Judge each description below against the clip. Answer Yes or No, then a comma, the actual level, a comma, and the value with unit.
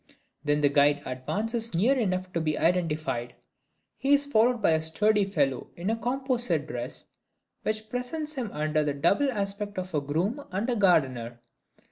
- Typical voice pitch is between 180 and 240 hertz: Yes, medium, 185 Hz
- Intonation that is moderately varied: No, wide, 7.3 semitones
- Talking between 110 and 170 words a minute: Yes, average, 165 wpm